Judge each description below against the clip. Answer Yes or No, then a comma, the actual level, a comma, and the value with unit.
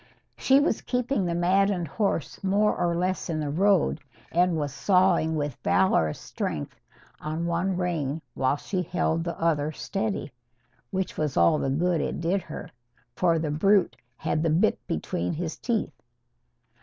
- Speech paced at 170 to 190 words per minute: No, average, 155 wpm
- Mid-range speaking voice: Yes, medium, 170 Hz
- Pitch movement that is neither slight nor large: Yes, average, 3.7 semitones